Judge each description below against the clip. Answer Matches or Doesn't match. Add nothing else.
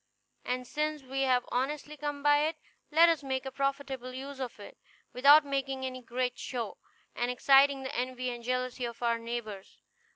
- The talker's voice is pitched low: Doesn't match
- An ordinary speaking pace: Matches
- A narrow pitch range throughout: Matches